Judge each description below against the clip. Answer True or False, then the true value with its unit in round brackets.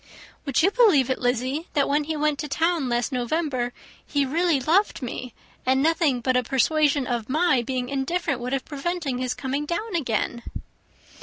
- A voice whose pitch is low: False (275 Hz)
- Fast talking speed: False (175 wpm)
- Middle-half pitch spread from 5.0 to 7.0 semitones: False (4.1 semitones)